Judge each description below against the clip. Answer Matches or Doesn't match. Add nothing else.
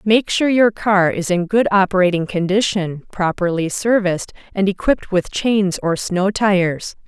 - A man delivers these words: Doesn't match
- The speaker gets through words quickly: Doesn't match